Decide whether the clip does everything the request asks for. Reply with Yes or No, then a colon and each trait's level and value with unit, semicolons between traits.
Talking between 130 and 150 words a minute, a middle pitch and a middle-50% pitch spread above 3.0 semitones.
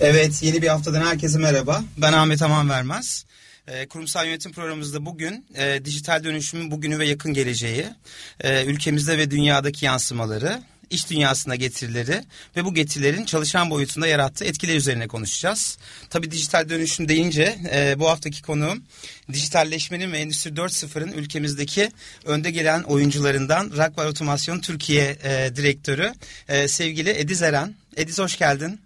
No: average, 135 wpm; medium, 155 Hz; narrow, 2.5 semitones